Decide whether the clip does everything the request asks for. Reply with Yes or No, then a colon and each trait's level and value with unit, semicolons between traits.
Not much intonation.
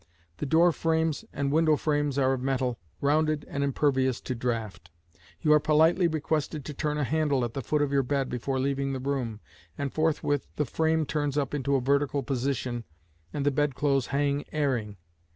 Yes: narrow, 2.3 semitones